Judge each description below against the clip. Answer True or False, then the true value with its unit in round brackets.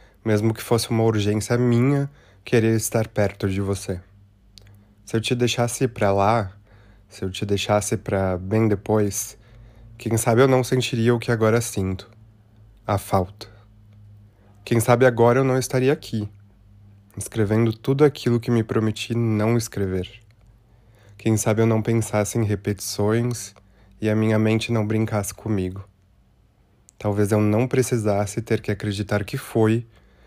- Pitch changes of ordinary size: False (2.3 semitones)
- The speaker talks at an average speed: True (145 wpm)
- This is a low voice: True (110 Hz)